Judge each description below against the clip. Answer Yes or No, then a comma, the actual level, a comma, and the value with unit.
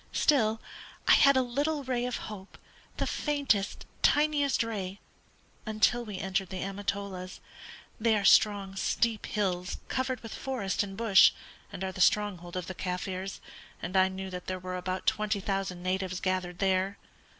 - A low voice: No, high, 195 Hz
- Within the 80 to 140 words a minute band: No, average, 160 wpm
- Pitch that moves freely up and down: No, average, 3.4 semitones